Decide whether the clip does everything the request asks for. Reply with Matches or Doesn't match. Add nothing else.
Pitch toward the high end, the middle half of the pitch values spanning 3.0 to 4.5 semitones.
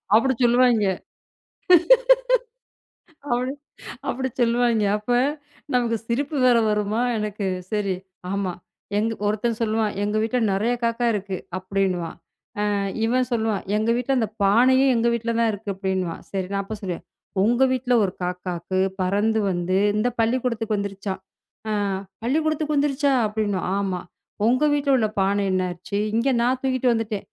Matches